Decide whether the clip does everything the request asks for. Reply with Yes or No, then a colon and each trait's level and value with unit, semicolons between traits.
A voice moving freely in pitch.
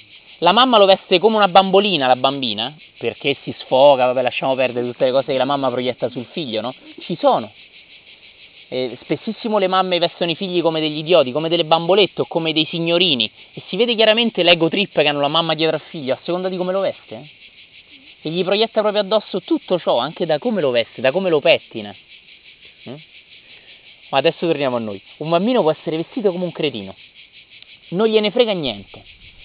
Yes: wide, 6.3 semitones